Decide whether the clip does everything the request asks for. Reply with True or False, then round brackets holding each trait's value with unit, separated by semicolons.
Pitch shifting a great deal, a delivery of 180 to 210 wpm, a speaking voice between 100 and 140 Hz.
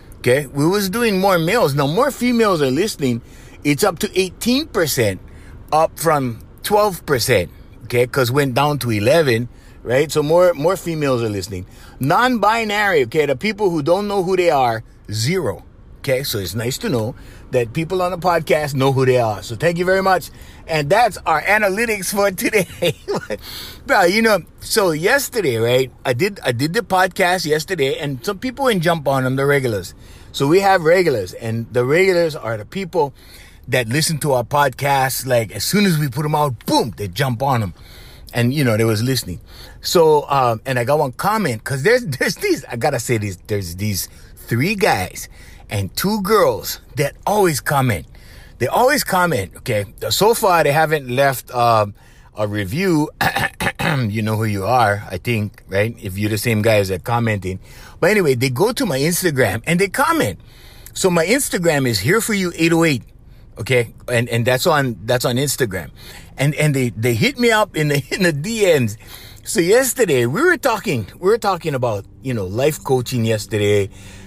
True (7.6 semitones; 185 wpm; 135 Hz)